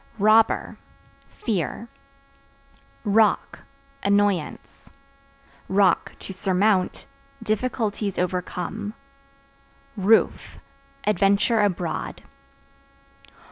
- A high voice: Yes, high, 205 Hz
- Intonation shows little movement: Yes, narrow, 2.3 semitones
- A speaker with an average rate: No, slow, 50 wpm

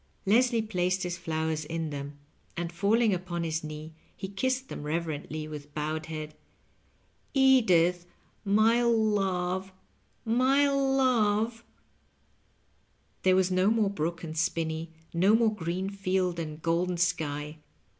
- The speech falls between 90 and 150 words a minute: Yes, slow, 135 wpm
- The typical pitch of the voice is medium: Yes, medium, 180 Hz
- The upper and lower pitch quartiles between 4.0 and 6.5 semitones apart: Yes, average, 5.2 semitones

